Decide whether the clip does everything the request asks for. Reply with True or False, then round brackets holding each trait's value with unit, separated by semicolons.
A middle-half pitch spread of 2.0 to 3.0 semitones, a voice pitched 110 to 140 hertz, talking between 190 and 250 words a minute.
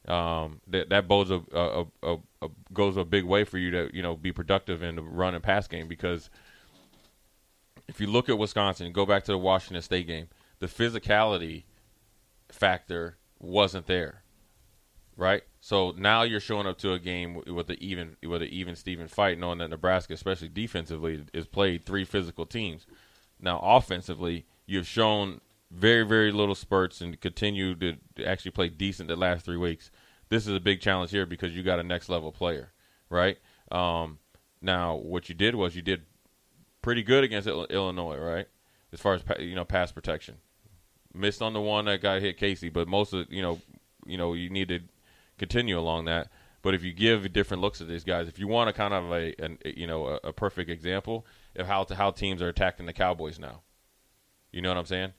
False (2.7 semitones; 95 Hz; 200 wpm)